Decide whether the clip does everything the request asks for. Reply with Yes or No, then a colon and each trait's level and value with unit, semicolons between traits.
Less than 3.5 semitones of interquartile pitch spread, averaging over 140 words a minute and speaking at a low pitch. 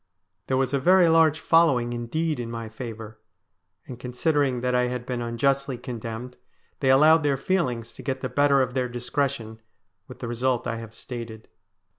Yes: average, 2.8 semitones; average, 175 wpm; low, 125 Hz